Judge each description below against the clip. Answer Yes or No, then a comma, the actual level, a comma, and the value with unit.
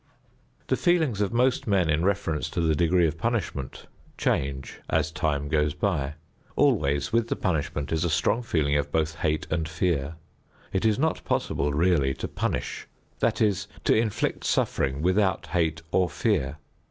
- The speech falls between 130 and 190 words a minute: Yes, average, 165 wpm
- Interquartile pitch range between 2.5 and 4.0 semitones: No, average, 5.1 semitones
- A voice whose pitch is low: Yes, very low, 80 Hz